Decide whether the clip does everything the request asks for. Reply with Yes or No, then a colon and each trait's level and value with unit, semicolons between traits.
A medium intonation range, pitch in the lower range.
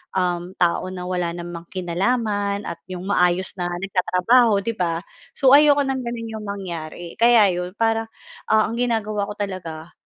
No: average, 4.2 semitones; high, 195 Hz